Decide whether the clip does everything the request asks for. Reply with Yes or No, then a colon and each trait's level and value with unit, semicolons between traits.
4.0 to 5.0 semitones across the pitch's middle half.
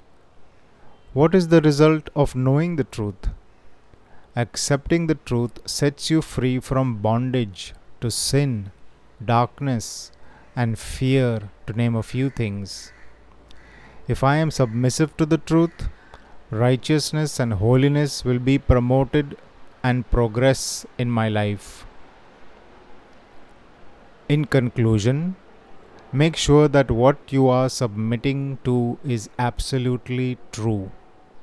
No: average, 3.6 semitones